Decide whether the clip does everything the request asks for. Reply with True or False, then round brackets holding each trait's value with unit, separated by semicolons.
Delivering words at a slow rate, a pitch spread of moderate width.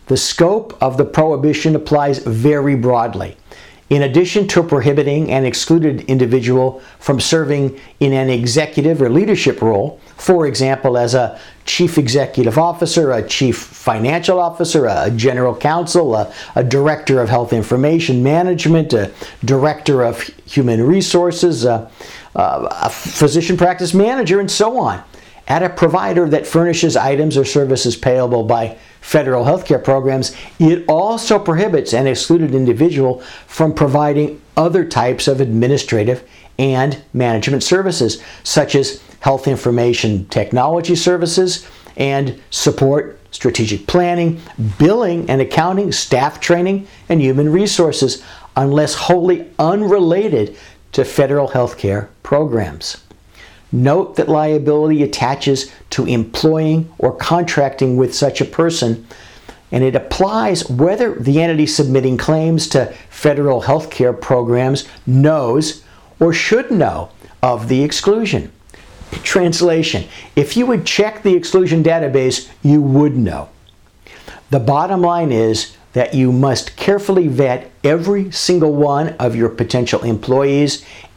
True (125 wpm; 4.7 semitones)